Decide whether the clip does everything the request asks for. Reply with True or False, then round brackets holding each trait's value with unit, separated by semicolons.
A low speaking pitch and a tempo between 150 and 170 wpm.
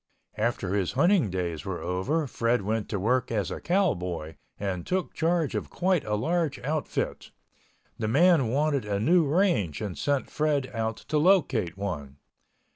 True (120 Hz; 160 wpm)